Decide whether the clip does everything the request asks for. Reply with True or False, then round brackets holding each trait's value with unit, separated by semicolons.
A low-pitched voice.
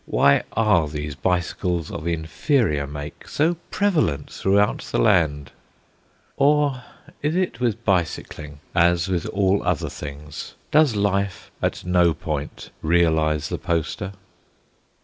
True (85 Hz)